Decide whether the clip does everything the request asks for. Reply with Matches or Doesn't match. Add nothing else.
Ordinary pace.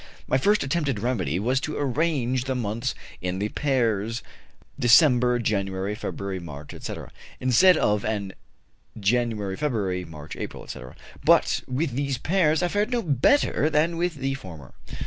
Matches